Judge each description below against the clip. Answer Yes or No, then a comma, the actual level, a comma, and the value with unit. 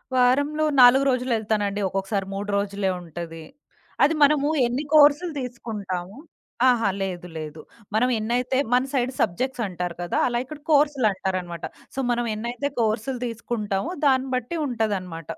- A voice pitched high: Yes, high, 230 Hz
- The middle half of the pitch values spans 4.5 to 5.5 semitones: Yes, average, 5.1 semitones